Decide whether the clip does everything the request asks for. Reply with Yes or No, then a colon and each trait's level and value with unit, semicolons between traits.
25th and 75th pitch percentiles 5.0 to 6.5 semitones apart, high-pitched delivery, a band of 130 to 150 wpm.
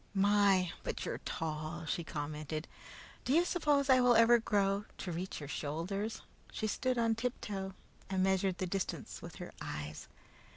No: wide, 5.4 semitones; high, 195 Hz; average, 160 wpm